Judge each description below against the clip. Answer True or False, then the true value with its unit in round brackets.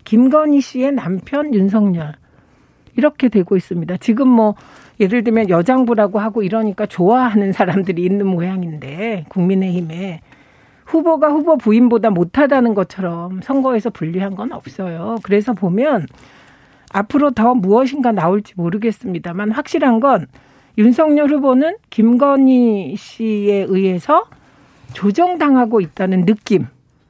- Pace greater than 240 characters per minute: True (295 characters per minute)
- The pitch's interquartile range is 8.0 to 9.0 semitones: False (5.3 semitones)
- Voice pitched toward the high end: True (215 Hz)